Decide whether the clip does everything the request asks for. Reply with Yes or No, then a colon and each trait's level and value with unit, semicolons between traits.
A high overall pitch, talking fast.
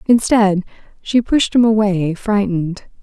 No: high, 205 Hz; slow, 100 wpm